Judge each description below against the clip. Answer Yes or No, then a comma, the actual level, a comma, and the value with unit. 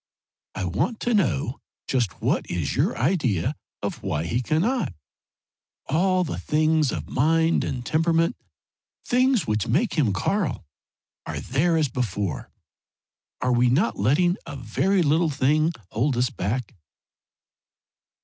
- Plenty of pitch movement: Yes, wide, 6.1 semitones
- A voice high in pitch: No, medium, 145 Hz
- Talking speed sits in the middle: No, slow, 130 wpm